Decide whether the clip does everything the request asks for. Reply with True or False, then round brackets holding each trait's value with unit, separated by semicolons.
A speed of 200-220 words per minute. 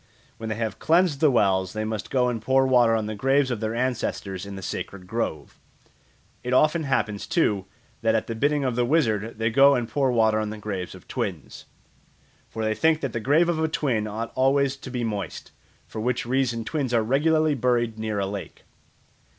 True (205 wpm)